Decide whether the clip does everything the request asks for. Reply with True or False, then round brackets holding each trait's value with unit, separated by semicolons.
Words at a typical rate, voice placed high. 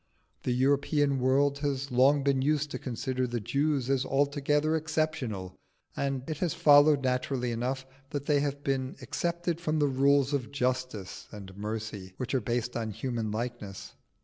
False (160 wpm; 135 Hz)